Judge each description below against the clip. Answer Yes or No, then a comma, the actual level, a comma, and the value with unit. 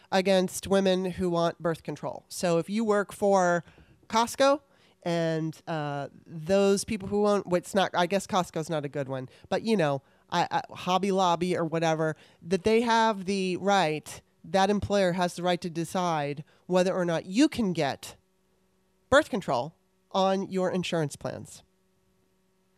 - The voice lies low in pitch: No, medium, 180 Hz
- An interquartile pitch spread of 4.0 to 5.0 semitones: No, average, 3.2 semitones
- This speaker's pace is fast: No, average, 160 wpm